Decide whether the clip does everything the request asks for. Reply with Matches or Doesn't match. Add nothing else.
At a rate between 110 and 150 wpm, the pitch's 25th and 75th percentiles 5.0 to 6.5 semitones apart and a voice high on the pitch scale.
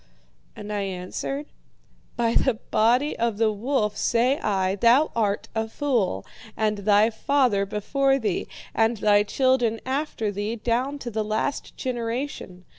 Doesn't match